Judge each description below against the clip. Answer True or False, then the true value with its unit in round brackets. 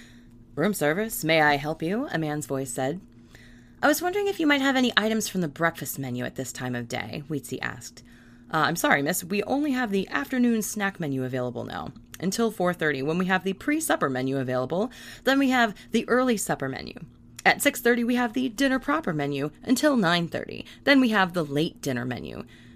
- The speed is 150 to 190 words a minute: False (200 wpm)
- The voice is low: False (170 Hz)